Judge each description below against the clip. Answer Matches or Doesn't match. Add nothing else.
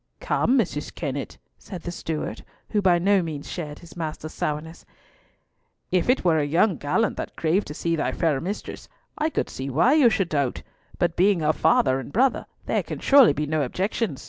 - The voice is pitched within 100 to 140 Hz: Doesn't match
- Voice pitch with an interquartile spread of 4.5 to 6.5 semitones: Matches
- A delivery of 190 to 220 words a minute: Matches